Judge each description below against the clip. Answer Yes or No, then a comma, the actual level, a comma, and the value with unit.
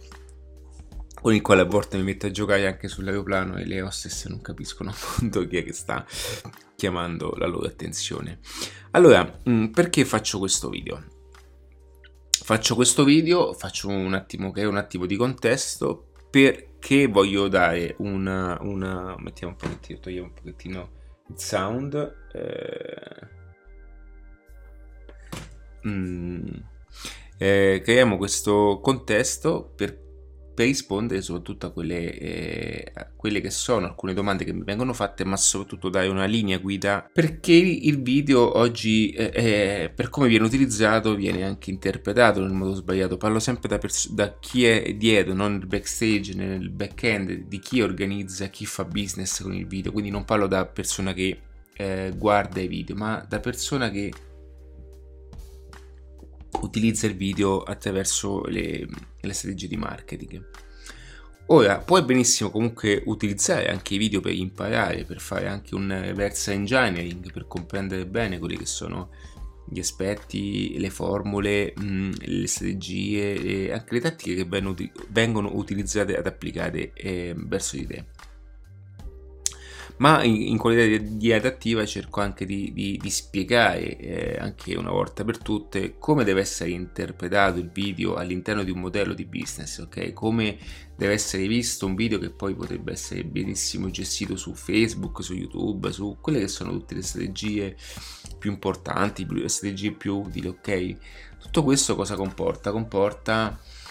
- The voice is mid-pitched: No, low, 100 Hz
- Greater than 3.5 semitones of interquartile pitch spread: No, average, 3.0 semitones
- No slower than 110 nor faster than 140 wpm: No, average, 150 wpm